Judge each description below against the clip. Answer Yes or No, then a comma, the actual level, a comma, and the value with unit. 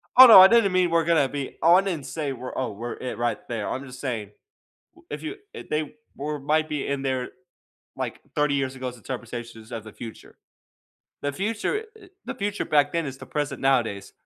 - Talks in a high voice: No, medium, 140 Hz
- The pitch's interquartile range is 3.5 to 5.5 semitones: Yes, average, 4.9 semitones